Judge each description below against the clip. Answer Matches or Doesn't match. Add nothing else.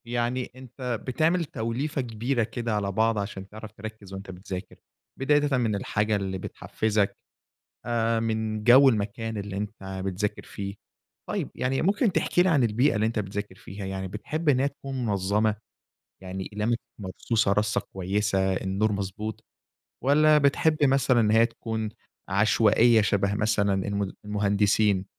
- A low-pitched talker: Matches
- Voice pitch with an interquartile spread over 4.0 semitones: Doesn't match